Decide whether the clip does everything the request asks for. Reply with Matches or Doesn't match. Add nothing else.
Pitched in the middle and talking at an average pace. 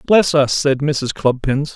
Matches